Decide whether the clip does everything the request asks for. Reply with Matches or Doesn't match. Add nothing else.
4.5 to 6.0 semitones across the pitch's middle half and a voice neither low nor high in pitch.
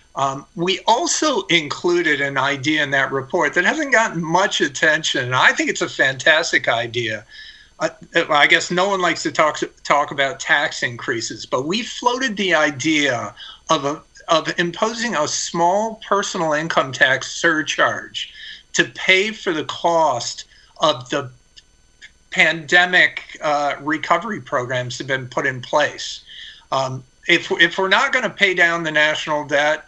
Matches